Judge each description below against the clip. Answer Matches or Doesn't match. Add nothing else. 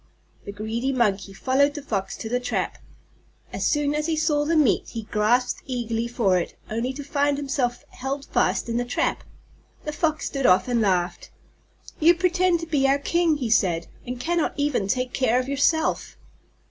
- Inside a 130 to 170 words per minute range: Doesn't match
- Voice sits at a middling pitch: Doesn't match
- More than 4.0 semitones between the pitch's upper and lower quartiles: Matches